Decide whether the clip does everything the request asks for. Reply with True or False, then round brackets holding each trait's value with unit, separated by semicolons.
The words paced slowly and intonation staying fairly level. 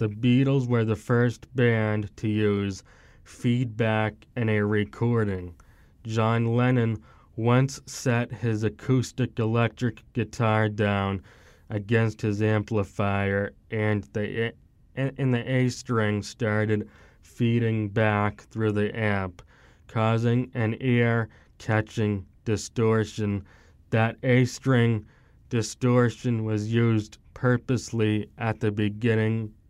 True (95 wpm; 2.1 semitones)